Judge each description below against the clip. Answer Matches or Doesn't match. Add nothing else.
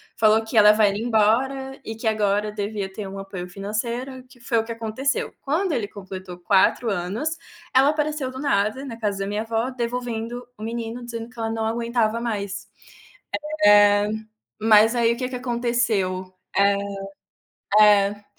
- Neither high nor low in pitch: Doesn't match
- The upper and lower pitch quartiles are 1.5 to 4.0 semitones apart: Matches